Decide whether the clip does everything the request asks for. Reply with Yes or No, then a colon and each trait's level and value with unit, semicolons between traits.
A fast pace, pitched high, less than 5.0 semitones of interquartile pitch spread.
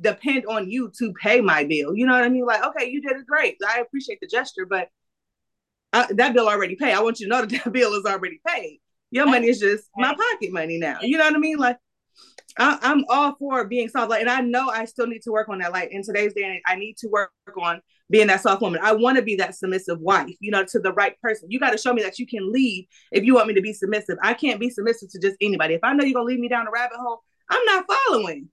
Yes: fast, 280 wpm; high, 225 Hz; average, 4.4 semitones